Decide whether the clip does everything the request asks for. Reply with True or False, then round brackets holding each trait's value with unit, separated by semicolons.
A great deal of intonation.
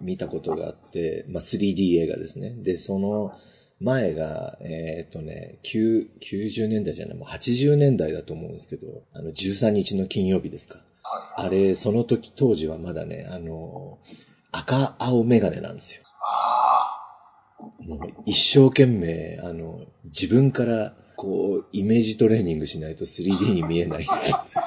True (5.7 semitones)